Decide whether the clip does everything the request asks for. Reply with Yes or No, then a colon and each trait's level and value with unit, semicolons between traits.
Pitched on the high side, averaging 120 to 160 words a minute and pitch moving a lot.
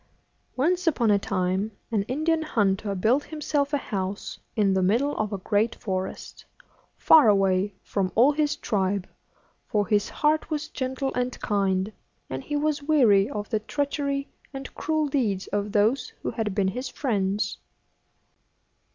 Yes: high, 220 Hz; average, 150 wpm; wide, 6.2 semitones